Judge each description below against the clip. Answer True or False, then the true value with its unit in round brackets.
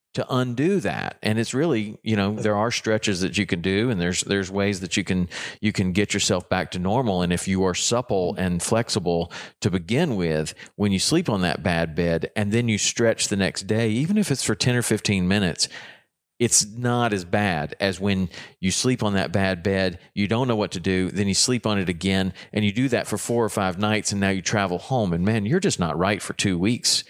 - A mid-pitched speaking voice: False (100 Hz)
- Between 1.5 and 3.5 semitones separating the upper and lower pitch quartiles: True (3.0 semitones)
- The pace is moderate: False (240 wpm)